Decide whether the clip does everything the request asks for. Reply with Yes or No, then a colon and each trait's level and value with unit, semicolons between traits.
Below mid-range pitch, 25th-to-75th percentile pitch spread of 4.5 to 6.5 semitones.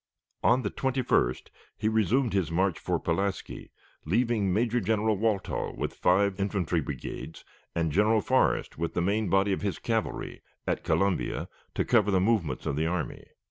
No: low, 100 Hz; average, 4.0 semitones